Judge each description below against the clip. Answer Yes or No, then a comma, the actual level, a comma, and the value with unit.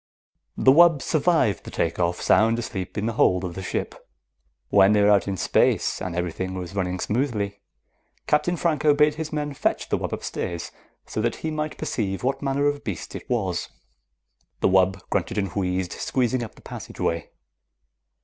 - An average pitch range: No, wide, 7.4 semitones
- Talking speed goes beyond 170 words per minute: Yes, average, 180 wpm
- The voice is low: Yes, low, 105 Hz